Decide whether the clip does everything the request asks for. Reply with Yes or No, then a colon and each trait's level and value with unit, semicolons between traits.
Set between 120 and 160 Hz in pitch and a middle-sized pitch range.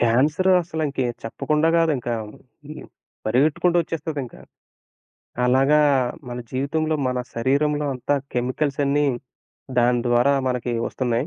Yes: medium, 140 Hz; average, 3.6 semitones